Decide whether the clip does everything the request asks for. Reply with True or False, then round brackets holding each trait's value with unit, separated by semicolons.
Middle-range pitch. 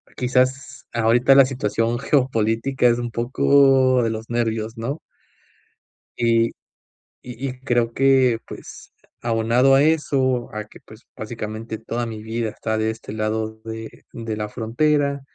False (120 Hz)